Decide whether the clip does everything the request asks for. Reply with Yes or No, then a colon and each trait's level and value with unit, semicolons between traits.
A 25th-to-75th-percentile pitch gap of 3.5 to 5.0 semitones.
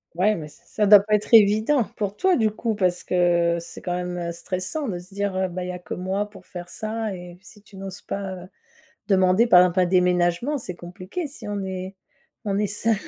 No: average, 2.8 semitones